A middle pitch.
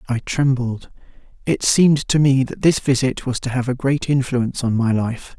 No: low, 130 Hz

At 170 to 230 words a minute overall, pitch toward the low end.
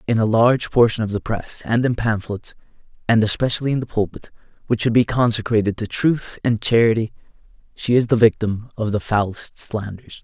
Yes: average, 180 wpm; low, 110 Hz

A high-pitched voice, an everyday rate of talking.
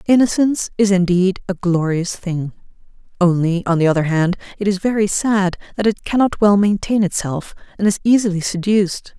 Yes: high, 195 Hz; average, 165 wpm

